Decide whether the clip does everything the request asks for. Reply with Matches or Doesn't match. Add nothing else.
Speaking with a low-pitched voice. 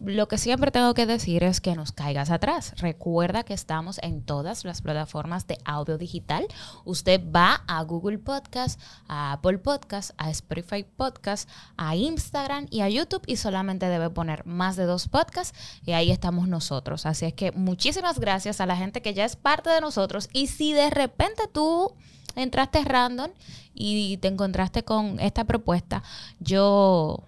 Doesn't match